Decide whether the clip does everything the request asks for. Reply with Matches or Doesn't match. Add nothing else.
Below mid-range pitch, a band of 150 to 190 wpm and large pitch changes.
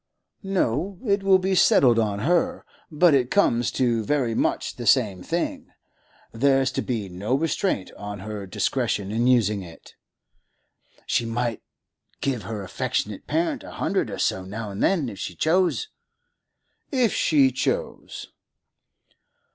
Doesn't match